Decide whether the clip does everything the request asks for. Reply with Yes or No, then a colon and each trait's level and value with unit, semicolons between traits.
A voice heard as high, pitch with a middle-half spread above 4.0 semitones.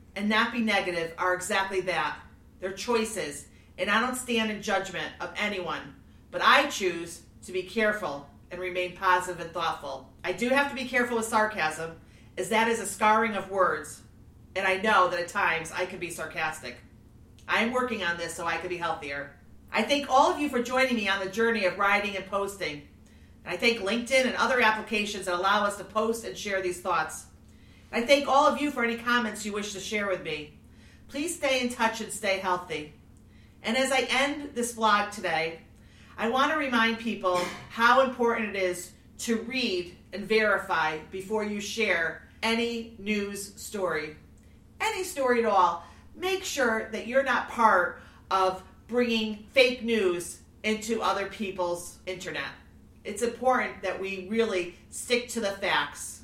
Yes: high, 205 Hz; average, 4.4 semitones